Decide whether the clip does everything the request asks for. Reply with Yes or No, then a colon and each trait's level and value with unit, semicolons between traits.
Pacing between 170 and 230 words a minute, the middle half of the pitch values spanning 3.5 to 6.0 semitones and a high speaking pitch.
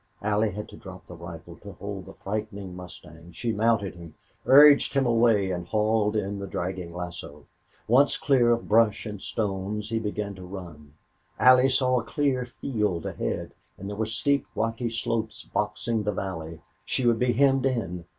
No: average, 175 wpm; average, 4.2 semitones; low, 105 Hz